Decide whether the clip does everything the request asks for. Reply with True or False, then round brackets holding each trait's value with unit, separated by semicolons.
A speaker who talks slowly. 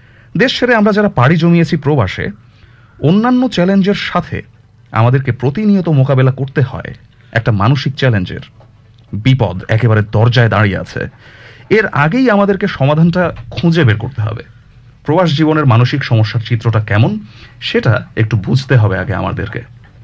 True (130 wpm)